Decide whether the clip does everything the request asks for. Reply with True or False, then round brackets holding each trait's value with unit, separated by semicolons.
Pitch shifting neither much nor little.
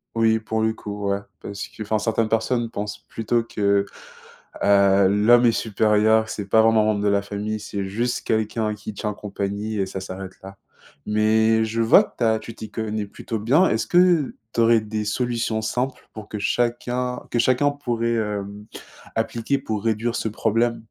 False (1.9 semitones)